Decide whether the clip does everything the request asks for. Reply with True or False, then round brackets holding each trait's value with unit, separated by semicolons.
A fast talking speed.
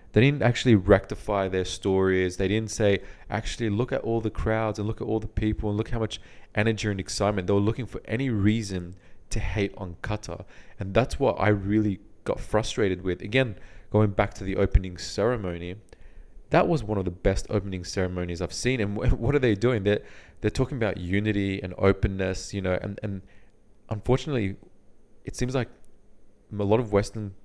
False (190 wpm)